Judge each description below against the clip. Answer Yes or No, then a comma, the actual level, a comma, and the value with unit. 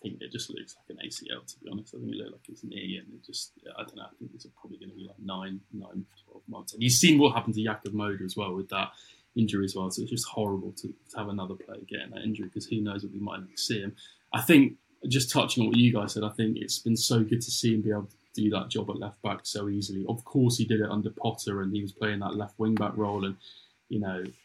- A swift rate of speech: Yes, fast, 295 wpm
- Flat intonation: Yes, narrow, 2.2 semitones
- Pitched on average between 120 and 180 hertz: No, low, 105 Hz